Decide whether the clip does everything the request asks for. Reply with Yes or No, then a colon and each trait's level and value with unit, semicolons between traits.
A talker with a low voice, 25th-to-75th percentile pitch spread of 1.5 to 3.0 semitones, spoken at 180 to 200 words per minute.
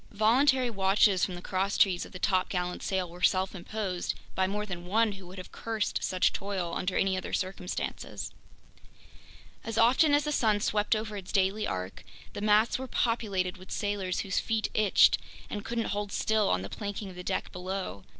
No: high, 195 Hz; average, 2.7 semitones; average, 185 wpm